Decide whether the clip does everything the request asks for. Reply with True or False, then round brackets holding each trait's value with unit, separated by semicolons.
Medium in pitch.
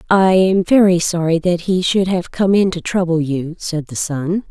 True (175 Hz)